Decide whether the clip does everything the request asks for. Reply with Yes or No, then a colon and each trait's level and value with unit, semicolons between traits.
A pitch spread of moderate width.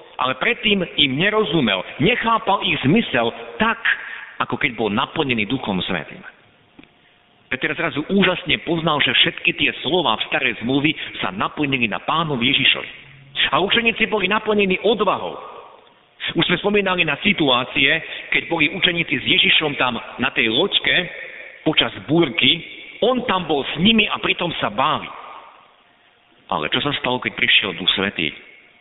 No: wide, 6.1 semitones